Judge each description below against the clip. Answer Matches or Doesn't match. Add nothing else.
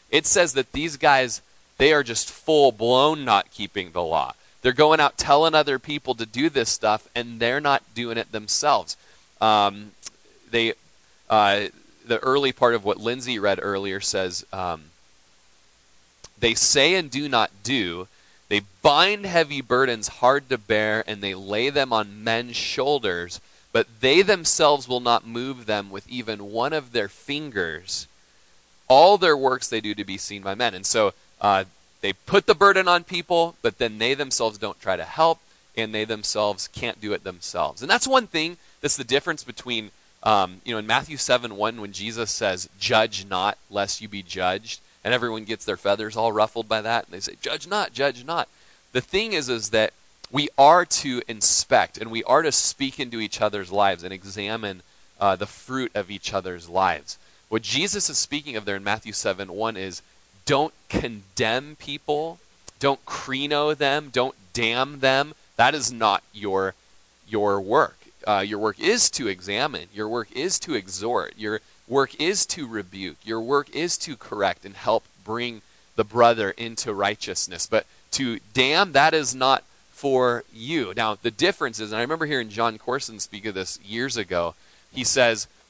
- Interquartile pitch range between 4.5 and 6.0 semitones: Matches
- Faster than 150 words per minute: Matches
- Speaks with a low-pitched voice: Matches